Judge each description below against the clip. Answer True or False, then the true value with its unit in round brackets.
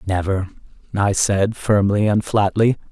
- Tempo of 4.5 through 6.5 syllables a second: False (4.2 syllables/s)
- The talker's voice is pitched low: True (100 Hz)